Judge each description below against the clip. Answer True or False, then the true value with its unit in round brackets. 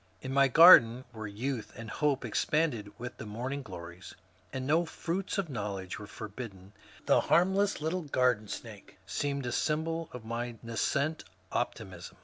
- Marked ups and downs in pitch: True (6.0 semitones)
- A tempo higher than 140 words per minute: True (155 wpm)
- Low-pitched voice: True (125 Hz)